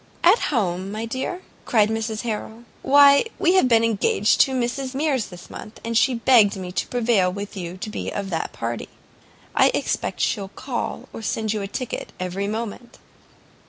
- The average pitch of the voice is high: Yes, high, 225 Hz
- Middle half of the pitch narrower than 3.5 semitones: No, average, 4.1 semitones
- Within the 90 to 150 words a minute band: No, average, 180 wpm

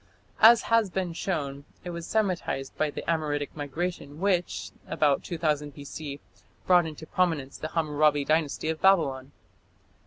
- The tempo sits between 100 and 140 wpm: Yes, slow, 135 wpm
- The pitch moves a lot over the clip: No, average, 3.4 semitones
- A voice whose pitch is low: No, medium, 155 Hz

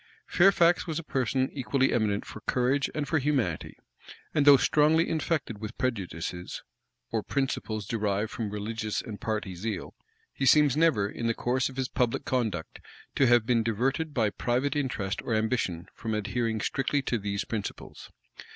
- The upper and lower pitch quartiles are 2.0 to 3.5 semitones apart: No, average, 4.5 semitones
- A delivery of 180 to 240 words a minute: No, average, 160 wpm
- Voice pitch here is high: No, low, 120 Hz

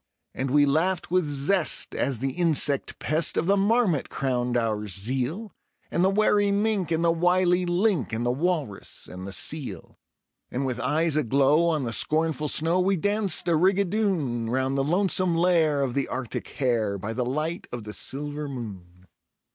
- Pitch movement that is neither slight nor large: No, wide, 6.1 semitones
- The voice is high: No, medium, 150 Hz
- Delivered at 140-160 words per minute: No, average, 170 wpm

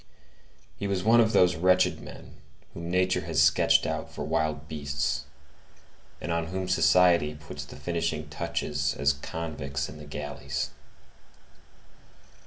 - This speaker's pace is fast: No, slow, 135 wpm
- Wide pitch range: No, average, 3.6 semitones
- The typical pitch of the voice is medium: No, very low, 80 Hz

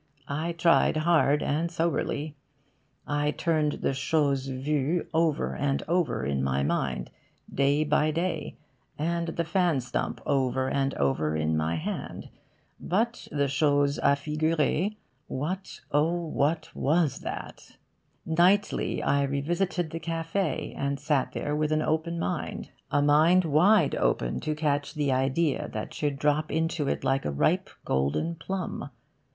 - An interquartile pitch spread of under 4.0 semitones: Yes, average, 3.1 semitones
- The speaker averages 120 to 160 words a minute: Yes, average, 140 wpm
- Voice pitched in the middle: Yes, medium, 150 Hz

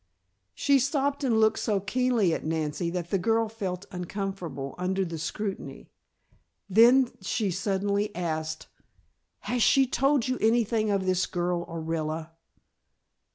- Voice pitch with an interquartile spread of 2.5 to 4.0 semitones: No, average, 4.8 semitones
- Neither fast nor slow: No, slow, 130 wpm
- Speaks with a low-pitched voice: No, high, 195 Hz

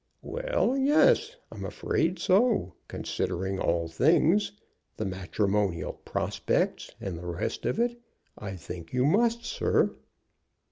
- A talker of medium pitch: No, low, 125 Hz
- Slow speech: Yes, slow, 120 wpm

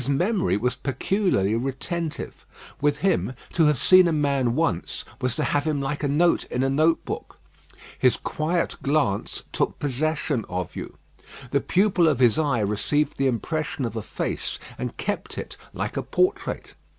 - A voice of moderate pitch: Yes, medium, 145 Hz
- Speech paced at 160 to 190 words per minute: Yes, average, 170 wpm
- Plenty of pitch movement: No, average, 4.3 semitones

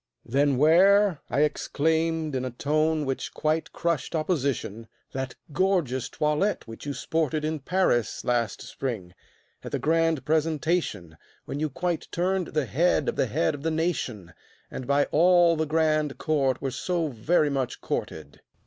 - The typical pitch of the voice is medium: Yes, medium, 155 Hz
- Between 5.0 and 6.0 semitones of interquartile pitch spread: No, average, 3.7 semitones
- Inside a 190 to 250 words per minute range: No, average, 155 wpm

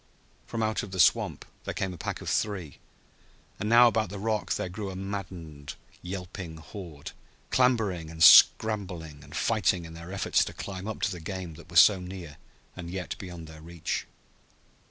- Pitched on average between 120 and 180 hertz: No, very low, 90 Hz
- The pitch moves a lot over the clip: No, average, 3.6 semitones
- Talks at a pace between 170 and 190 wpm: Yes, average, 180 wpm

